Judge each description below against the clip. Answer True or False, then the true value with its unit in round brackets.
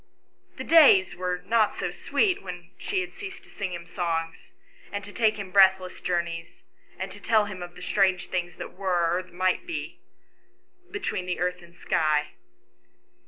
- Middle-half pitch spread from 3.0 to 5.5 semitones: False (2.6 semitones)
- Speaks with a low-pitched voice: False (185 Hz)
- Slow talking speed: False (170 wpm)